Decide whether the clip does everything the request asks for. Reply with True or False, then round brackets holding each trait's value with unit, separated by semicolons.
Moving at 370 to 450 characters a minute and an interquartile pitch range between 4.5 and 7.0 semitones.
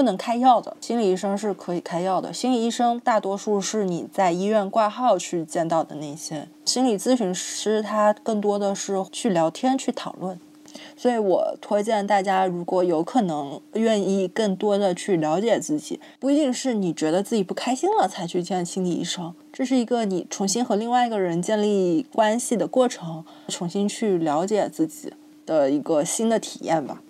False (285 characters per minute; 5.1 semitones)